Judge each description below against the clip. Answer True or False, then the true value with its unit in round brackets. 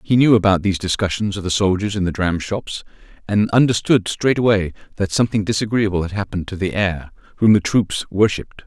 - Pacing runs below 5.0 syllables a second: False (5.8 syllables/s)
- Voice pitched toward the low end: True (100 Hz)